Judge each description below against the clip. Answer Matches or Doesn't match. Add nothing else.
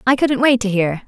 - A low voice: Doesn't match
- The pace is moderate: Doesn't match